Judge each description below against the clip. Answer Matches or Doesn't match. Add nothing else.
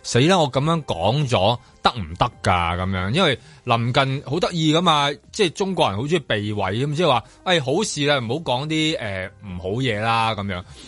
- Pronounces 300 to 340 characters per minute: Doesn't match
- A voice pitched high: Doesn't match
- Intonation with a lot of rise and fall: Matches